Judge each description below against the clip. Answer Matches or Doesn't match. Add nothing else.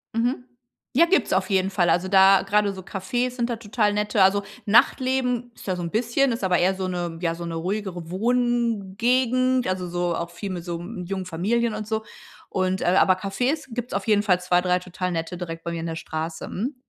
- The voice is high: Matches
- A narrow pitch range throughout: Doesn't match